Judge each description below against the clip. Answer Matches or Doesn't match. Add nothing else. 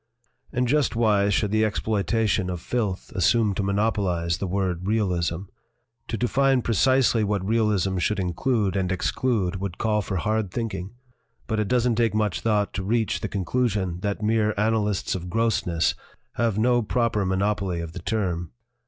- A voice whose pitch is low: Matches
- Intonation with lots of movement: Doesn't match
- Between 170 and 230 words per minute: Doesn't match